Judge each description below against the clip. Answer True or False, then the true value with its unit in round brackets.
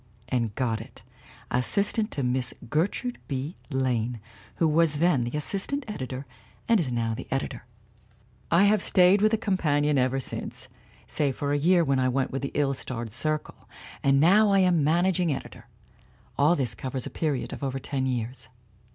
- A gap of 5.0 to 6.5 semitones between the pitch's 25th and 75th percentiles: True (5.4 semitones)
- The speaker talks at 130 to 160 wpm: False (175 wpm)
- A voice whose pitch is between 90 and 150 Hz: True (140 Hz)